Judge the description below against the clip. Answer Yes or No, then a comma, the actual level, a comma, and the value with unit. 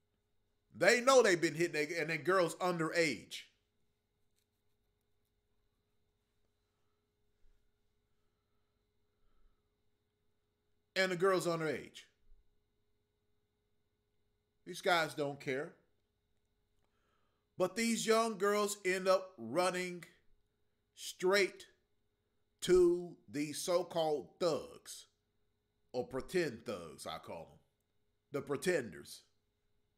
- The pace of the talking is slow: Yes, slow, 80 wpm